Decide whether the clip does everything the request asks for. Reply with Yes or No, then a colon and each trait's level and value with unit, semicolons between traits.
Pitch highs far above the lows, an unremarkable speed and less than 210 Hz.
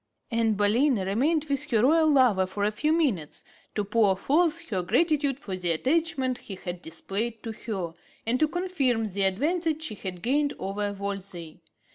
No: wide, 7.2 semitones; average, 170 wpm; high, 225 Hz